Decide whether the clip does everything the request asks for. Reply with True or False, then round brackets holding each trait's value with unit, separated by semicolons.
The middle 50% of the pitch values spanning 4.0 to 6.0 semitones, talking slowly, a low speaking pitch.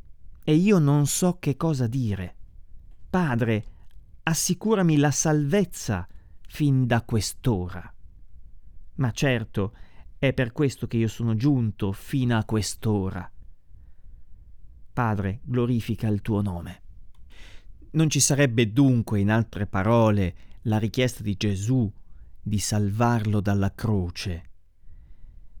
True (5.6 semitones; 110 wpm; 105 Hz)